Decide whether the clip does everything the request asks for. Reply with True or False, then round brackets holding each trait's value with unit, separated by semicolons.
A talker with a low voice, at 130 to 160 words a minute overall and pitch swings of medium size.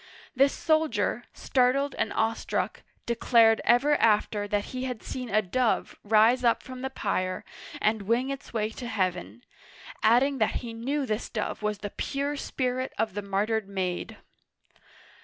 False (230 Hz; 155 wpm; 3.4 semitones)